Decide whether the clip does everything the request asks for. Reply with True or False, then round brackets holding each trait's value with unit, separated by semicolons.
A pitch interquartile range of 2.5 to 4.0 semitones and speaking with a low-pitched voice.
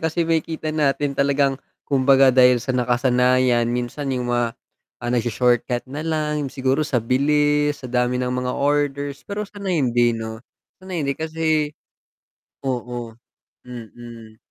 True (3.3 semitones; 130 Hz)